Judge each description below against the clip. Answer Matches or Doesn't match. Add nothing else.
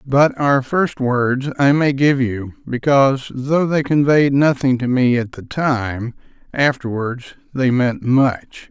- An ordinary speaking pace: Matches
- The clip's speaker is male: Matches